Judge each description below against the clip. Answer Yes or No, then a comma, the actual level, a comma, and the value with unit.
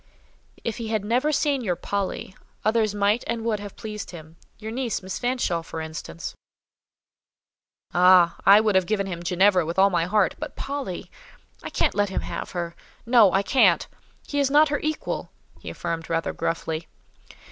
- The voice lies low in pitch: No, high, 200 Hz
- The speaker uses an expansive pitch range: No, average, 4.7 semitones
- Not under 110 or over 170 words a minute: Yes, average, 165 wpm